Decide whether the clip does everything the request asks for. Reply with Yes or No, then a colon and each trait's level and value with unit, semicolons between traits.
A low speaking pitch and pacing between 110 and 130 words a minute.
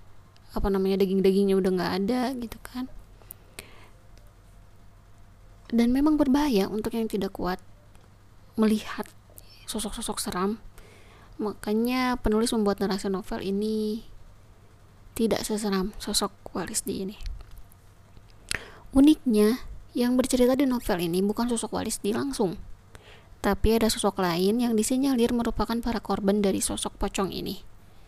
No: high, 200 Hz; average, 115 wpm